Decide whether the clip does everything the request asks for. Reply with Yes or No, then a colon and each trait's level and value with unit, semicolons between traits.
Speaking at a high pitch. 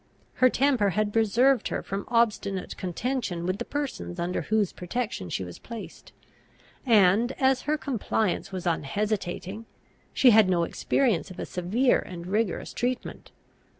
Yes: high, 210 Hz